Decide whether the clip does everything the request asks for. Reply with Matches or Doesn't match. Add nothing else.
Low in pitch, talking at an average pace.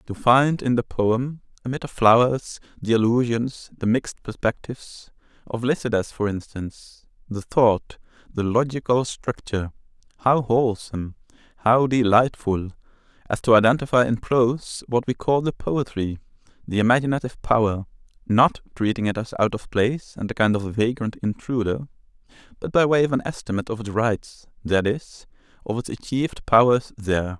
Matches